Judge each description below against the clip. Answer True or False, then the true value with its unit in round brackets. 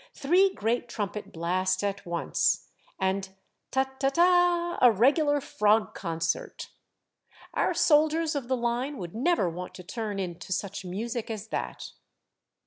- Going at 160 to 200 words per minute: False (150 wpm)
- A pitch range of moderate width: False (7.3 semitones)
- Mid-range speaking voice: False (225 Hz)